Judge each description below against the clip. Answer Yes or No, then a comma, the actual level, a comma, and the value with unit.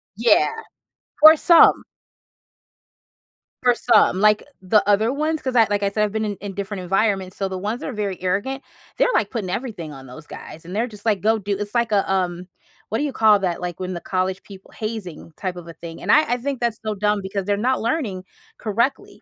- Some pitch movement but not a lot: Yes, average, 3.8 semitones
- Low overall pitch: No, high, 205 Hz